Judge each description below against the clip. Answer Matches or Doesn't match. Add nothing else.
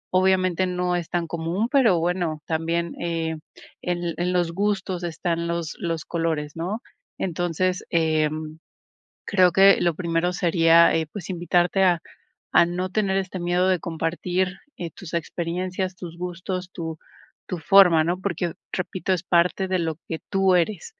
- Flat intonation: Matches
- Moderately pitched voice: Matches